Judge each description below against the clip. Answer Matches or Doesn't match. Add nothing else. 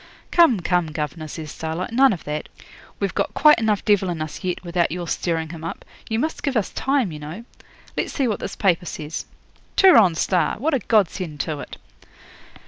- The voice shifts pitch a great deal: Matches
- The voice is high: Doesn't match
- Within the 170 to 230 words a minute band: Matches